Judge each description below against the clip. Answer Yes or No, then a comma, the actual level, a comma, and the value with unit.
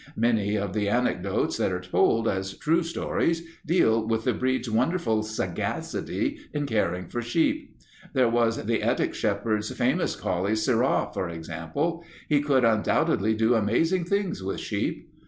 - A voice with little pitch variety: No, average, 5.3 semitones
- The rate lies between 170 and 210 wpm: No, average, 150 wpm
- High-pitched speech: No, low, 115 Hz